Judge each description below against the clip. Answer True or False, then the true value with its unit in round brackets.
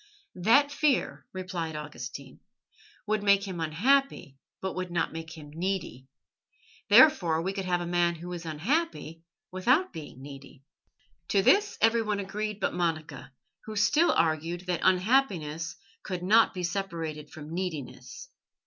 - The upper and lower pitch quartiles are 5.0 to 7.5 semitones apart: False (4.4 semitones)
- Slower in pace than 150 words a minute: True (140 wpm)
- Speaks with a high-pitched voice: False (180 Hz)